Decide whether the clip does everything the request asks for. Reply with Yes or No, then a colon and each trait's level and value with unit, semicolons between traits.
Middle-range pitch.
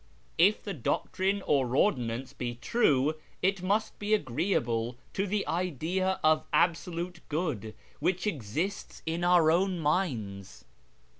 Yes: medium, 165 Hz